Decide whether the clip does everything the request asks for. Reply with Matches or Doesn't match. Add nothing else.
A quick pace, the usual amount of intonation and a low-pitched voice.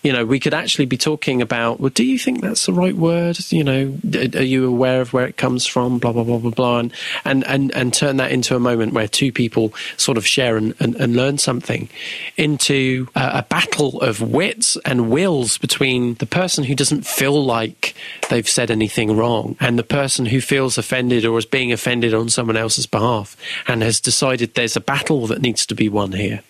Matches